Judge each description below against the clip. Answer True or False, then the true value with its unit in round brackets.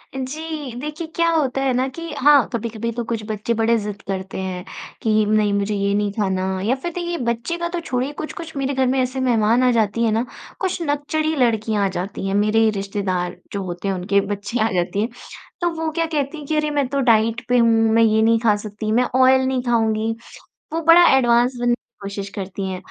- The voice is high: True (230 Hz)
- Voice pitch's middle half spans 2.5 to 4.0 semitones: False (4.7 semitones)